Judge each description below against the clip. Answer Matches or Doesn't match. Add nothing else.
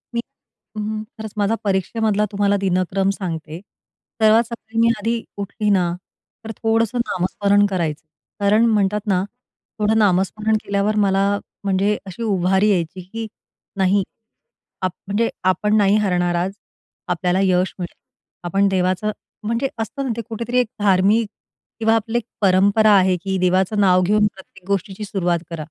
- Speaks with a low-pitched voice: Doesn't match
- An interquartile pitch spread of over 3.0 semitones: Doesn't match